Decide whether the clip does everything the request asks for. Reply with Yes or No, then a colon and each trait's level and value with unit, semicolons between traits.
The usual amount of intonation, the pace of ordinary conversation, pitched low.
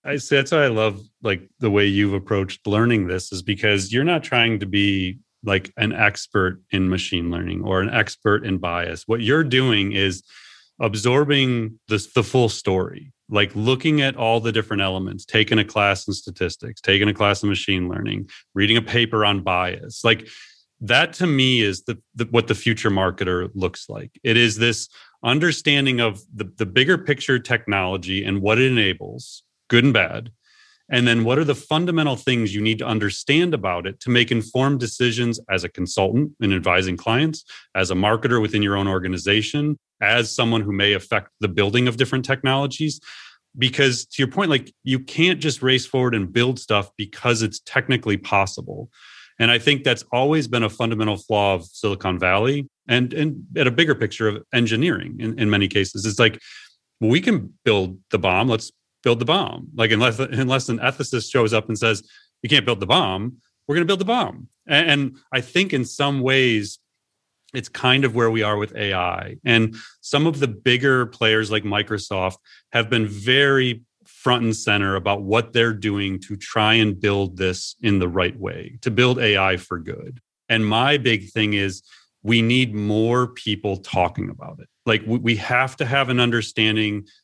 Yes: average, 4.1 semitones; average, 190 wpm; low, 110 Hz